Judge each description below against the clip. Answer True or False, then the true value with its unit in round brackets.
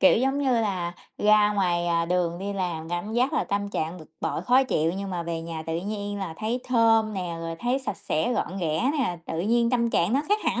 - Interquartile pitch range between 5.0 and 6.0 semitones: True (5.4 semitones)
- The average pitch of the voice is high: True (200 Hz)